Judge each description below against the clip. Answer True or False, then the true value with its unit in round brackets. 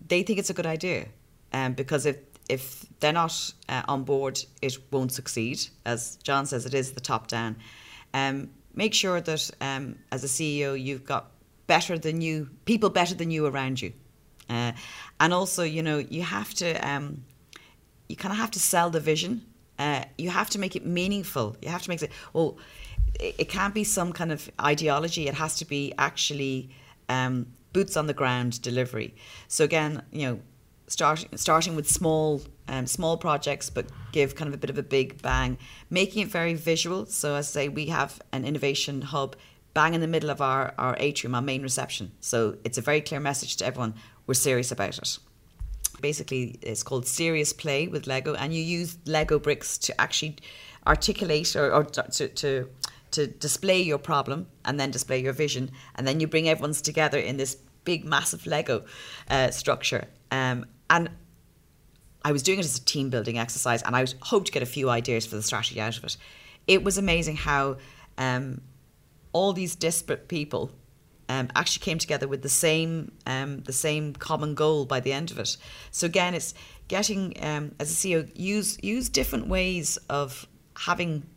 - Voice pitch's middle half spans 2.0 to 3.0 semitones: False (3.7 semitones)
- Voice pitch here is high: False (145 Hz)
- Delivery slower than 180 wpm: False (190 wpm)